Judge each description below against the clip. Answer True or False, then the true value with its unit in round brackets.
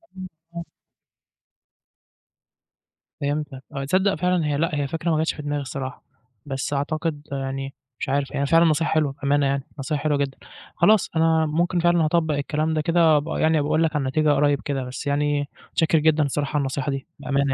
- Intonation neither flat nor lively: False (2.3 semitones)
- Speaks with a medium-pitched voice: True (150 Hz)